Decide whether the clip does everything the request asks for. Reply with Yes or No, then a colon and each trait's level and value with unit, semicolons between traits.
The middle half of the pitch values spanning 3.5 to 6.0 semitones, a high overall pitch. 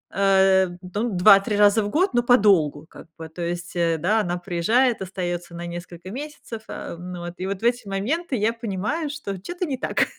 Yes: average, 5.1 semitones; high, 195 Hz